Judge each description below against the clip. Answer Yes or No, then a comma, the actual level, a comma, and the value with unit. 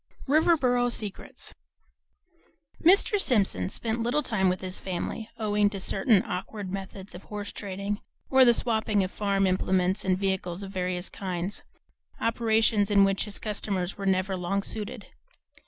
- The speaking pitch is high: Yes, high, 200 Hz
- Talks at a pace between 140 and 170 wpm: Yes, average, 150 wpm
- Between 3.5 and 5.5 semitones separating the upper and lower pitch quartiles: No, average, 2.8 semitones